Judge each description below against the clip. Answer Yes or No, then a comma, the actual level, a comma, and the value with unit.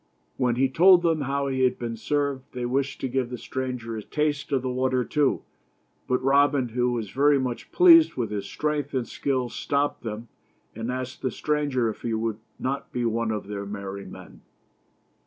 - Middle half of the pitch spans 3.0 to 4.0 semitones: Yes, average, 3.3 semitones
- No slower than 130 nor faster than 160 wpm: No, average, 195 wpm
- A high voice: No, low, 130 Hz